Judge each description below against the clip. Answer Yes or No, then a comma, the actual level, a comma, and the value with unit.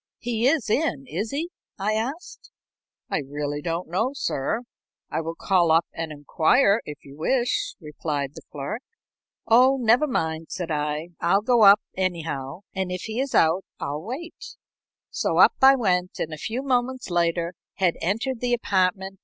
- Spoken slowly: No, average, 165 wpm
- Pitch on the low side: No, high, 190 Hz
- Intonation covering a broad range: Yes, wide, 7.1 semitones